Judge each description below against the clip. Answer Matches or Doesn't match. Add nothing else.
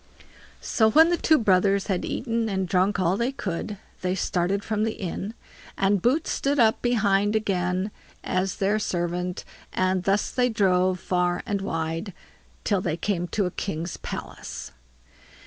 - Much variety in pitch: Doesn't match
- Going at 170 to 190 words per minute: Doesn't match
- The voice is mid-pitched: Doesn't match